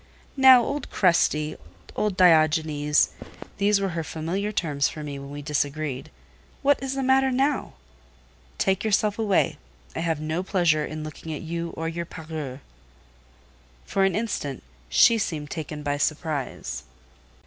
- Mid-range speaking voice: Yes, medium, 165 Hz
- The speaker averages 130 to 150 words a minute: Yes, average, 140 wpm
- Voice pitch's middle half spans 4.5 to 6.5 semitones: Yes, average, 5.1 semitones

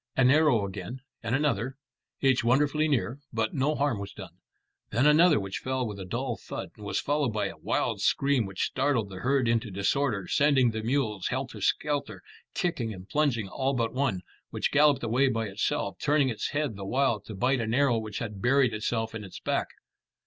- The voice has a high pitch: No, low, 120 Hz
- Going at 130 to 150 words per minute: No, average, 200 wpm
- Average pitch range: Yes, average, 4.6 semitones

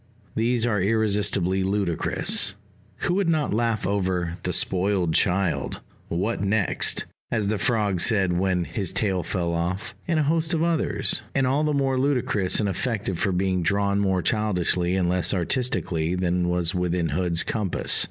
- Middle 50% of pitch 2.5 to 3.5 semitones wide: No, average, 4.0 semitones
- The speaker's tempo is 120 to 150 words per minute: No, average, 160 wpm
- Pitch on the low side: Yes, low, 100 Hz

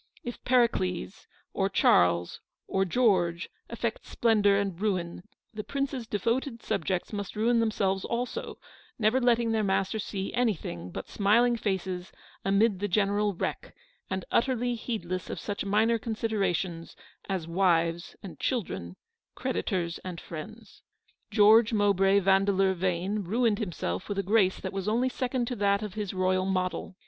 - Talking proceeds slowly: No, average, 145 wpm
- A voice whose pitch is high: Yes, high, 200 Hz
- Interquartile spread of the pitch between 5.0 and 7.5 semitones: No, average, 3.5 semitones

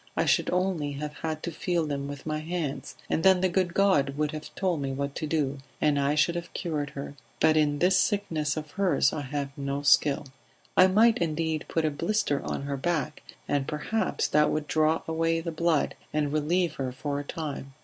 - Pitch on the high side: No, medium, 155 Hz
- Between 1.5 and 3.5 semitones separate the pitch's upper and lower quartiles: Yes, average, 3.0 semitones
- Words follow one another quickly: Yes, fast, 210 wpm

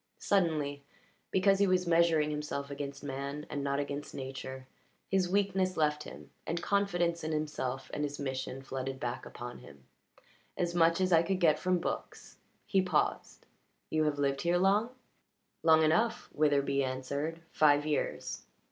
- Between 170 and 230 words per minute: No, average, 155 wpm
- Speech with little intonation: No, average, 4.0 semitones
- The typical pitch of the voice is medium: Yes, medium, 150 Hz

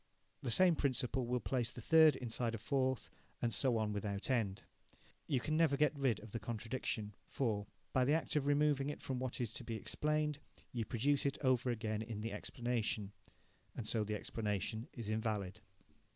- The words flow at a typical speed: Yes, average, 185 wpm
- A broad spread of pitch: No, average, 4.0 semitones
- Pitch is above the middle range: No, low, 120 Hz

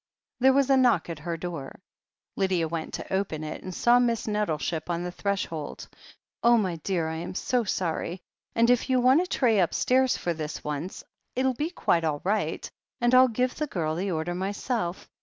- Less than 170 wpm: No, average, 195 wpm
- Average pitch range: No, wide, 6.6 semitones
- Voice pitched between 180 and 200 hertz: Yes, high, 190 Hz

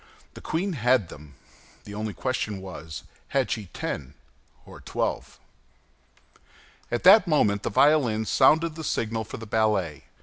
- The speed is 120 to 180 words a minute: Yes, average, 140 wpm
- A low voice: Yes, low, 110 Hz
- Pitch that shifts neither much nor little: No, wide, 5.8 semitones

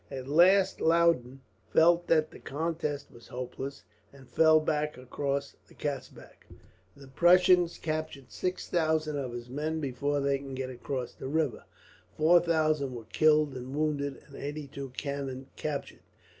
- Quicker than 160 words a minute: No, average, 150 wpm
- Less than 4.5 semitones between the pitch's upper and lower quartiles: Yes, average, 2.8 semitones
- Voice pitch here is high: No, medium, 145 Hz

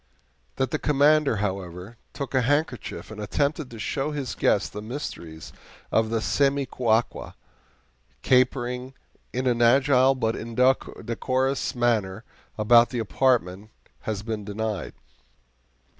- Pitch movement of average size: Yes, average, 3.7 semitones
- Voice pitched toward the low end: Yes, low, 120 Hz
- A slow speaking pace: Yes, slow, 115 wpm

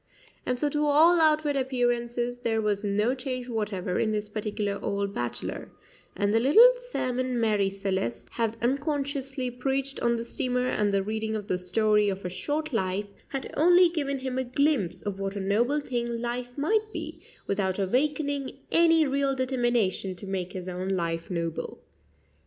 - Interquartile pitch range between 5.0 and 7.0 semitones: Yes, wide, 5.5 semitones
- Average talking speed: Yes, average, 170 wpm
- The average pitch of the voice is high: Yes, high, 240 Hz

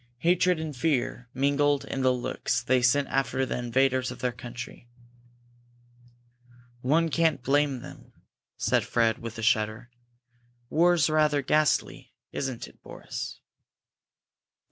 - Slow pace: Yes, slow, 120 wpm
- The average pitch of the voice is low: Yes, low, 130 Hz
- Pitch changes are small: No, average, 3.5 semitones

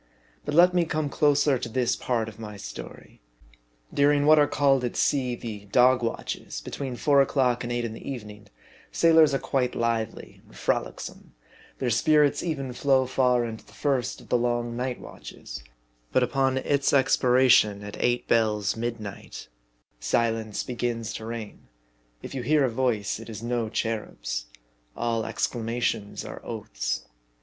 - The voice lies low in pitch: Yes, low, 120 Hz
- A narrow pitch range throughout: No, average, 3.3 semitones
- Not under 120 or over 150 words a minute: No, average, 160 wpm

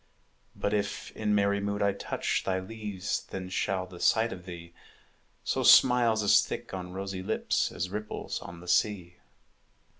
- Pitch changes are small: Yes, narrow, 2.2 semitones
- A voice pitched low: Yes, low, 100 Hz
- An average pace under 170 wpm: Yes, average, 160 wpm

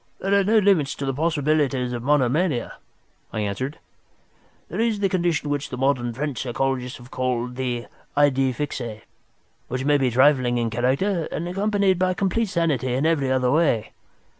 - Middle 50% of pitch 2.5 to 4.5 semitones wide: No, average, 5.2 semitones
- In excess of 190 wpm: No, average, 165 wpm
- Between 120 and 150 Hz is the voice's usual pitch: Yes, medium, 140 Hz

